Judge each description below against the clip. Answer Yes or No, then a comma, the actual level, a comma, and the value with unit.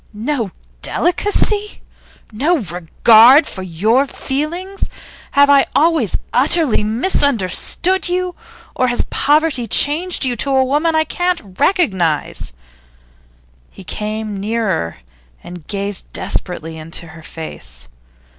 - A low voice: No, very high, 250 Hz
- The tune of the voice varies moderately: No, wide, 8.4 semitones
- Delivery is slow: Yes, slow, 110 wpm